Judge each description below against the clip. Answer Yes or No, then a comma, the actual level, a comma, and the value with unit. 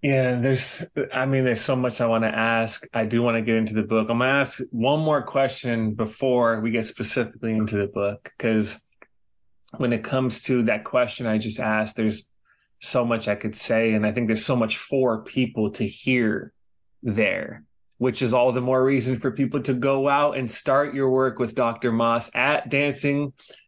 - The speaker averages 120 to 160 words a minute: No, fast, 205 wpm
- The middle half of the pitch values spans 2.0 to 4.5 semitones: Yes, average, 2.8 semitones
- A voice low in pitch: Yes, low, 125 Hz